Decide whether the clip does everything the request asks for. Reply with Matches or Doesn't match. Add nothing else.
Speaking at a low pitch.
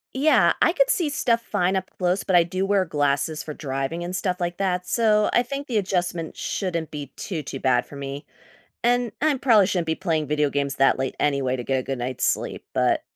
Doesn't match